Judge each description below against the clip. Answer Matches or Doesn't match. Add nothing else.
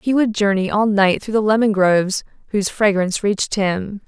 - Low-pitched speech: Doesn't match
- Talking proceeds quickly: Doesn't match